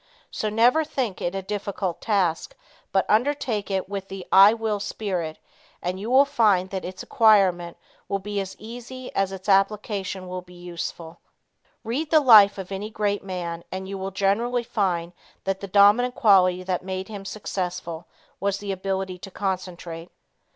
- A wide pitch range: No, narrow, 2.5 semitones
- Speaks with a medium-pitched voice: No, high, 195 Hz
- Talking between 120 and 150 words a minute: No, average, 165 wpm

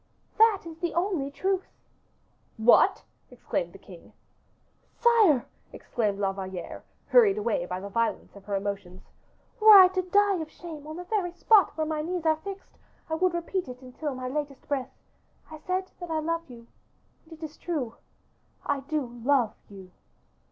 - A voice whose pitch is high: Yes, very high, 315 Hz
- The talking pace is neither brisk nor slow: Yes, average, 170 wpm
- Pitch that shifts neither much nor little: No, wide, 6.8 semitones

